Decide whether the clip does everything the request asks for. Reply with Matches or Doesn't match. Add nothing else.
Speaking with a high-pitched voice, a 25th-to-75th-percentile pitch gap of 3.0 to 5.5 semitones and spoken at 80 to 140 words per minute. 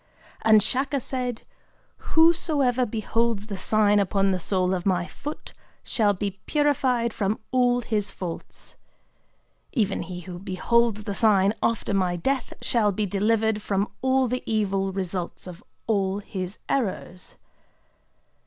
Matches